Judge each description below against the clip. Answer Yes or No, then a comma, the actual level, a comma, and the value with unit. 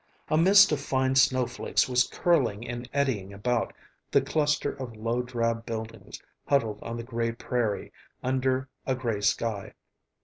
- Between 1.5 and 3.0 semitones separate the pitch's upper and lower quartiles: Yes, narrow, 2.5 semitones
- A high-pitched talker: No, low, 125 Hz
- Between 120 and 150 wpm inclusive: Yes, average, 145 wpm